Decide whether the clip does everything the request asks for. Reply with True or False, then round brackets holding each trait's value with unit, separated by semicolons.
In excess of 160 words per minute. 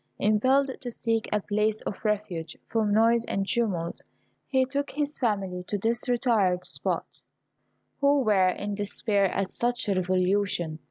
False (150 wpm)